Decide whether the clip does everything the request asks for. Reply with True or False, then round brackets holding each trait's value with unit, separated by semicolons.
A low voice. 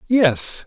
False (190 Hz)